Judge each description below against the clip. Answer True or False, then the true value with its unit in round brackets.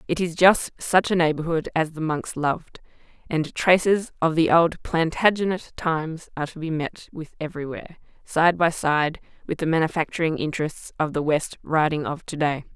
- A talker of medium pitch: True (160 Hz)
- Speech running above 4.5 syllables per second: True (5.2 syllables/s)